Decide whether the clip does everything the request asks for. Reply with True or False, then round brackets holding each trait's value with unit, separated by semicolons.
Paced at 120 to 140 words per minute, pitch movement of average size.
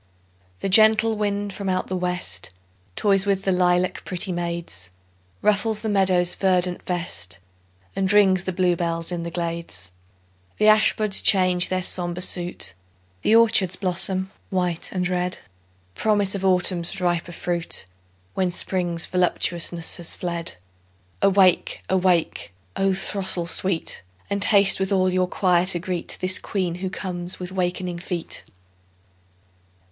False (135 wpm; 1.7 semitones)